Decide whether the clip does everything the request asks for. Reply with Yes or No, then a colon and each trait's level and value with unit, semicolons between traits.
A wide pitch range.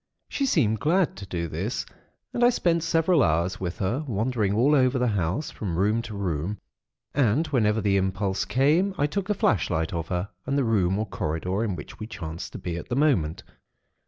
Yes: wide, 7.5 semitones